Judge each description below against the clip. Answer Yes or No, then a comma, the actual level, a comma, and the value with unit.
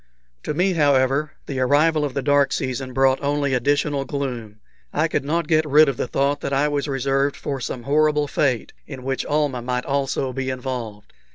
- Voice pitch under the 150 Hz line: Yes, medium, 140 Hz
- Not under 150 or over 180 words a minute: No, average, 190 wpm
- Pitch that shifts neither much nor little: No, narrow, 2.1 semitones